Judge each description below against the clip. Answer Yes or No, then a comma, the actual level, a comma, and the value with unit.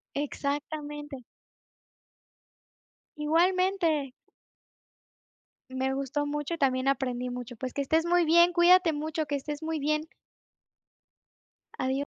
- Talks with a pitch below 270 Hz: No, very high, 295 Hz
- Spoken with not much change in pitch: No, average, 3.0 semitones